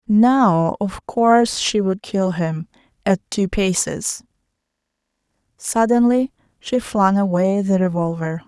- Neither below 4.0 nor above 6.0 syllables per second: No, 3.7 syllables/s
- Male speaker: No, female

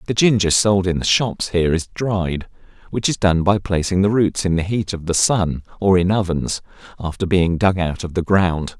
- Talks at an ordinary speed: No, fast, 220 wpm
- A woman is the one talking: No, male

